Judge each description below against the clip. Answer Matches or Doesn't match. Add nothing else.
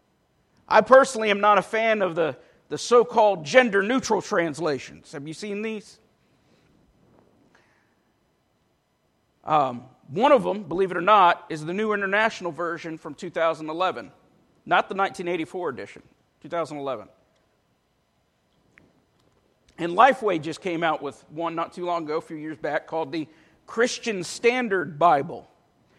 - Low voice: Doesn't match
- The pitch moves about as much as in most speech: Matches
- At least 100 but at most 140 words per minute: Matches